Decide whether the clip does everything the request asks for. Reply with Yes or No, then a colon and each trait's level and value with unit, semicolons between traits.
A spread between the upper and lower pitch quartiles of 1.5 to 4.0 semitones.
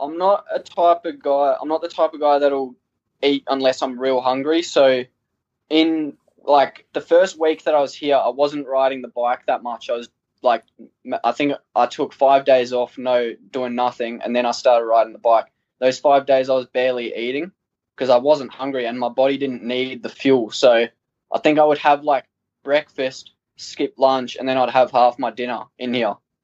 Yes: average, 2.9 semitones